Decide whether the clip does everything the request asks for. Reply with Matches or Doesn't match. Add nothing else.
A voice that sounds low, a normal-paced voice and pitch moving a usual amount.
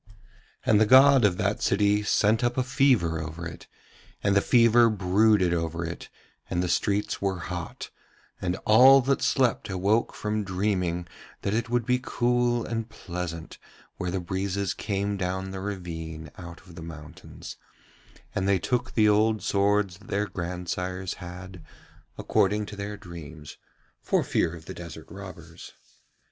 Matches